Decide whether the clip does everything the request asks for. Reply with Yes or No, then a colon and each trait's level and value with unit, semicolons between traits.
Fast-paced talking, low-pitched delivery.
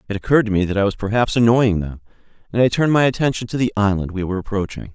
Yes: fast, 255 wpm; low, 105 Hz